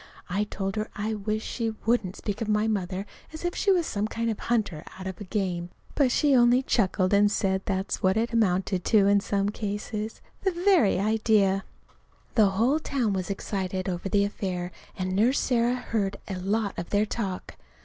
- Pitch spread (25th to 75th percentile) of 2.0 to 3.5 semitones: Yes, average, 3.0 semitones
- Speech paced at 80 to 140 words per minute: No, average, 195 wpm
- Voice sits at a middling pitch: No, high, 205 Hz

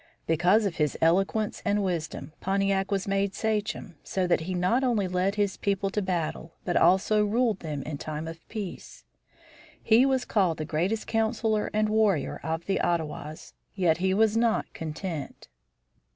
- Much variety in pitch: No, average, 4.3 semitones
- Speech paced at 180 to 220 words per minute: No, average, 165 wpm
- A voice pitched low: No, high, 190 Hz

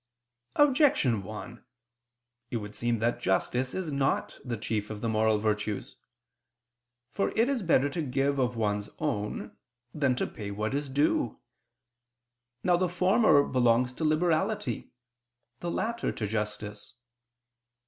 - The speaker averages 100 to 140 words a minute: Yes, slow, 135 wpm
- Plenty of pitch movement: Yes, wide, 7.5 semitones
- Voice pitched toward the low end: Yes, low, 125 Hz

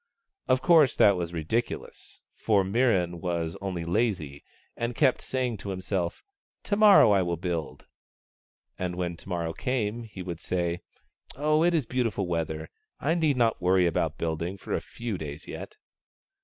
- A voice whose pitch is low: Yes, very low, 95 Hz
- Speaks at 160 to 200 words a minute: Yes, average, 170 wpm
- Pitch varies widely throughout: Yes, wide, 6.0 semitones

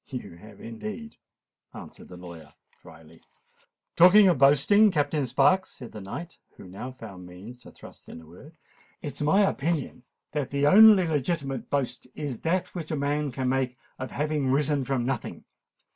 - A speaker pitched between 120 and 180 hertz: Yes, medium, 140 Hz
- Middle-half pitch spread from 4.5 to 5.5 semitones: Yes, average, 4.8 semitones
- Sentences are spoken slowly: No, average, 170 wpm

